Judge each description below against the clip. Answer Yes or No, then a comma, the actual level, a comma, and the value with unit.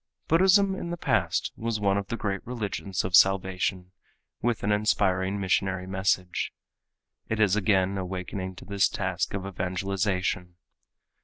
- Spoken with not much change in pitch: Yes, narrow, 2.1 semitones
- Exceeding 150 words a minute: No, average, 140 wpm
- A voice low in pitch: Yes, very low, 95 Hz